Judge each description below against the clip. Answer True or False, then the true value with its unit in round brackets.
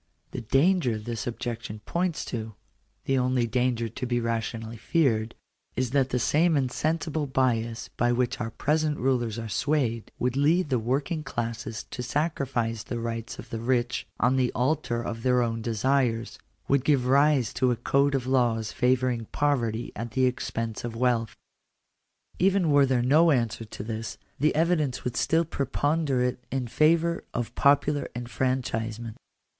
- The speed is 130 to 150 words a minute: False (160 wpm)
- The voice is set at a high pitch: False (125 Hz)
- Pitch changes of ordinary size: True (3.4 semitones)